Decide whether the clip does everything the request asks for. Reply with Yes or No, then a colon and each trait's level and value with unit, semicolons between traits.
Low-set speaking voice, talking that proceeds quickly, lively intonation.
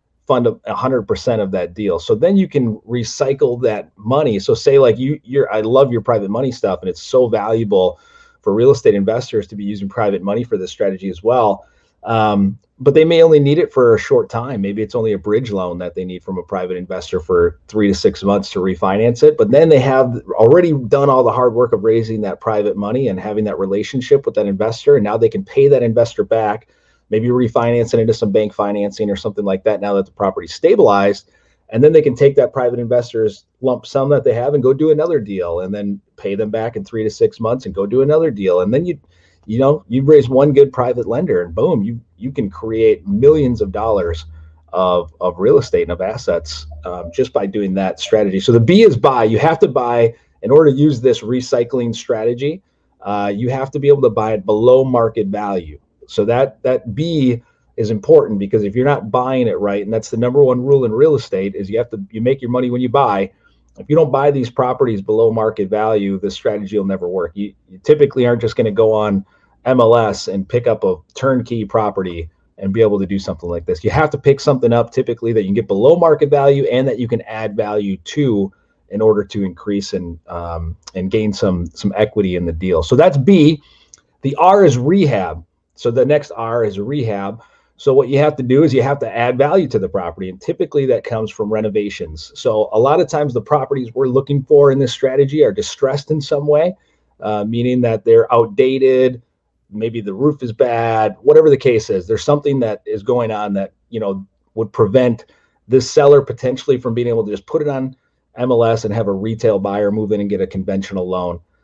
Yes: low, 115 Hz; fast, 225 wpm; wide, 5.9 semitones